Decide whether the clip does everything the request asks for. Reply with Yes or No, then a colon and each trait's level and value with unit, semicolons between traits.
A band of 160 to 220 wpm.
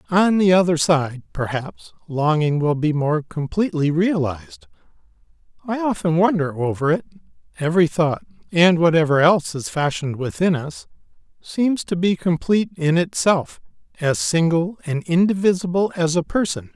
No: slow, 135 wpm